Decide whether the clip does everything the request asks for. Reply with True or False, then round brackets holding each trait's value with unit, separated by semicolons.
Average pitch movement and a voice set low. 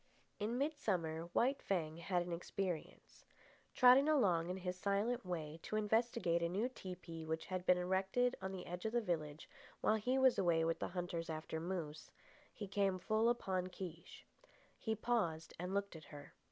False (4.5 semitones; 185 Hz)